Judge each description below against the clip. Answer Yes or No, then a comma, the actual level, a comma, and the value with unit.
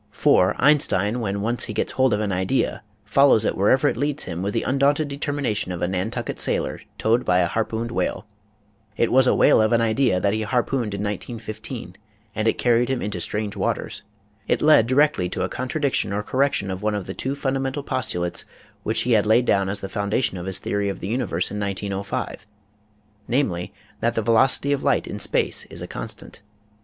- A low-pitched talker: Yes, low, 110 Hz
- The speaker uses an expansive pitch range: No, average, 4.7 semitones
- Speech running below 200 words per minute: No, fast, 205 wpm